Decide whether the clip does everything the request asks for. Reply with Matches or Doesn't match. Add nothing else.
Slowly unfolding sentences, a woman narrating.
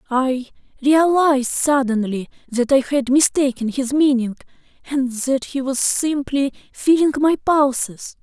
Matches